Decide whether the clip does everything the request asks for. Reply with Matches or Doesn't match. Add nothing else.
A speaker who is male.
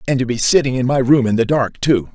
Matches